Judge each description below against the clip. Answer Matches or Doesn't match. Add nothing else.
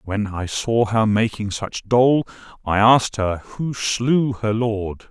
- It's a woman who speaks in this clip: Doesn't match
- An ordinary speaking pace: Matches